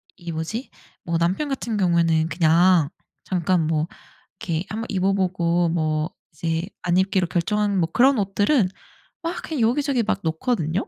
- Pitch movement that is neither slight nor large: Yes, average, 4.1 semitones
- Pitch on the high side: No, medium, 180 Hz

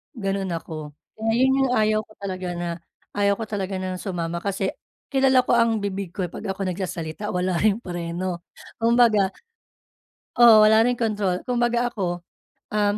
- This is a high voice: Yes, high, 200 Hz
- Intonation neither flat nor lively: Yes, average, 3.6 semitones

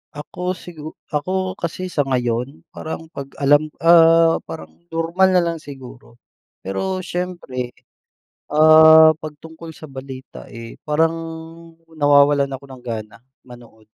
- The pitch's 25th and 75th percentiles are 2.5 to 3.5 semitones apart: No, average, 3.9 semitones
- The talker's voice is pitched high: No, medium, 155 Hz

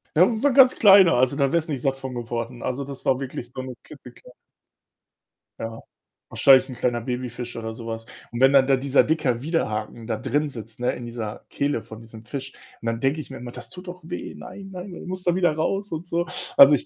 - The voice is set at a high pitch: No, low, 135 Hz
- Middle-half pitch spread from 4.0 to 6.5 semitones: Yes, average, 5.2 semitones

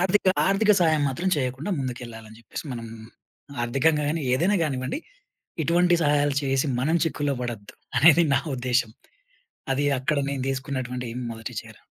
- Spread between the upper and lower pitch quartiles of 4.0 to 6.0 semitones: Yes, average, 4.4 semitones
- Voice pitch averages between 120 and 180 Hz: Yes, low, 135 Hz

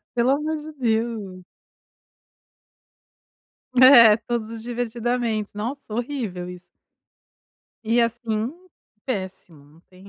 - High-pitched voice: Yes, high, 230 Hz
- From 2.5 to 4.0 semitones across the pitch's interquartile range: Yes, average, 2.8 semitones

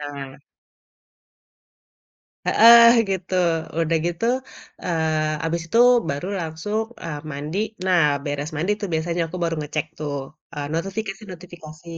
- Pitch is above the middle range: No, medium, 165 Hz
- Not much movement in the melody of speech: No, average, 3.2 semitones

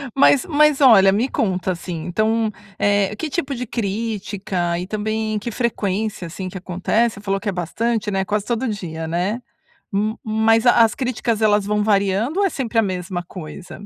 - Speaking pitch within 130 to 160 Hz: No, high, 210 Hz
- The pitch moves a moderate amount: Yes, average, 3.2 semitones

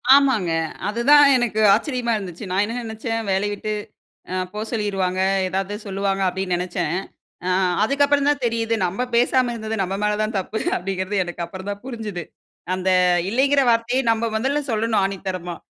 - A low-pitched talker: No, high, 210 Hz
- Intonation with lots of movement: No, average, 3.8 semitones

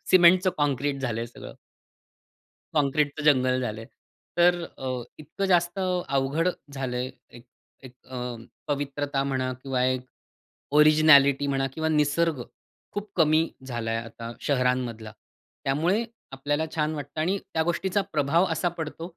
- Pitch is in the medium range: Yes, medium, 145 Hz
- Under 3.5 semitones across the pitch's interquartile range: No, average, 3.8 semitones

